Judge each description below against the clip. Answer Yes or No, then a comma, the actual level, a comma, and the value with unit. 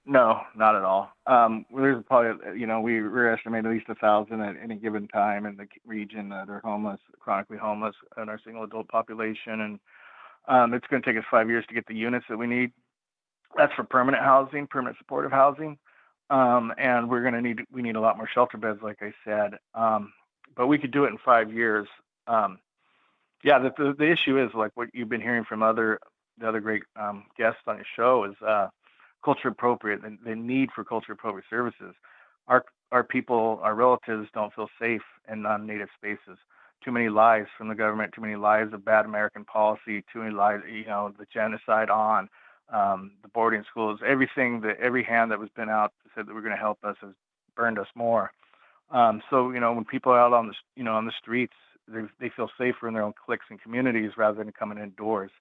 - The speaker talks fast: Yes, fast, 210 wpm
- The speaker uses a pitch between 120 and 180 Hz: No, low, 110 Hz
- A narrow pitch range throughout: Yes, narrow, 2.2 semitones